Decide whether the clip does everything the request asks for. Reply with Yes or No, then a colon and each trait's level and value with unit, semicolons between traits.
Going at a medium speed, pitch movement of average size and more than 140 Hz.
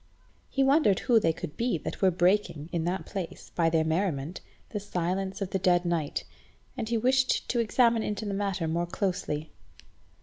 Yes: average, 180 wpm; average, 4.3 semitones; high, 190 Hz